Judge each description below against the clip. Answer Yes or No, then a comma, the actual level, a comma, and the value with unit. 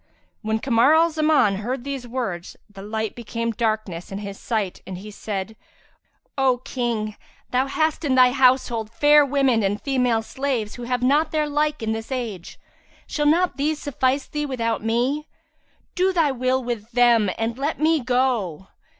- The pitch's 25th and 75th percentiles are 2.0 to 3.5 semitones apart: No, average, 4.2 semitones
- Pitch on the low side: No, high, 245 Hz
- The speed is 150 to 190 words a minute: Yes, average, 170 wpm